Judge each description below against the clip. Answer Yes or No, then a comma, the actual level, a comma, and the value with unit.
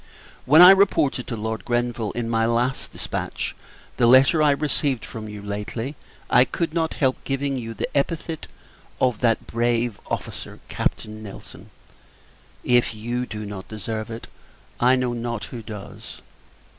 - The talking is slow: No, average, 150 wpm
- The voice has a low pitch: Yes, low, 120 Hz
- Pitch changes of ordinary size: Yes, average, 3.1 semitones